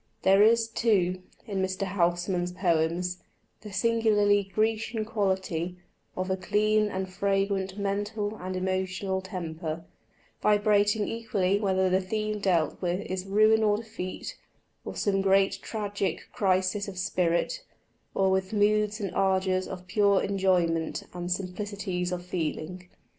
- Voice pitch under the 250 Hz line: Yes, high, 190 Hz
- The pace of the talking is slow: Yes, slow, 130 wpm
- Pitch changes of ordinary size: No, narrow, 2.1 semitones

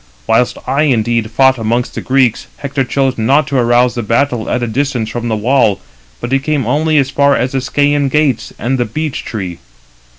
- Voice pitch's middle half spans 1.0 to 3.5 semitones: Yes, average, 3.1 semitones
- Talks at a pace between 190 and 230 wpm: Yes, average, 200 wpm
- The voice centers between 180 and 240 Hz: No, low, 125 Hz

